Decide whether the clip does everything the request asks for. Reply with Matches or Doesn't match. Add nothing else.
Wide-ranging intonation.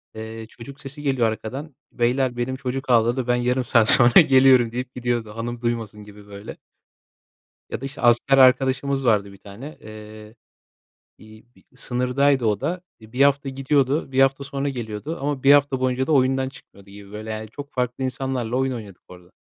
Doesn't match